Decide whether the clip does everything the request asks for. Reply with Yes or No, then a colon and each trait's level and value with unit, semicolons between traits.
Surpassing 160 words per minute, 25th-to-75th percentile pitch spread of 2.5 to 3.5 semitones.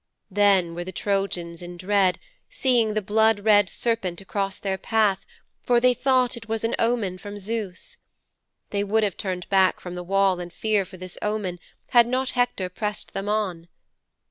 Yes: average, 175 wpm; average, 3.1 semitones